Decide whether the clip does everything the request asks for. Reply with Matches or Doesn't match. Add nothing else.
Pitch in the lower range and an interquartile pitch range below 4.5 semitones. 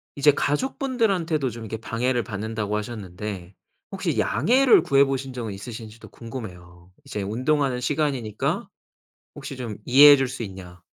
Doesn't match